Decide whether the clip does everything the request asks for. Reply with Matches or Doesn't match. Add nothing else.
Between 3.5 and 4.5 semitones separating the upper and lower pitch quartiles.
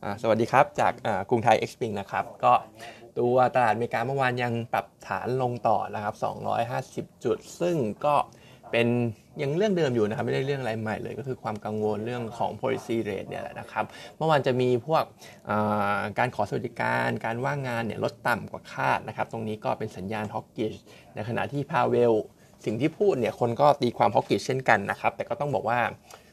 Doesn't match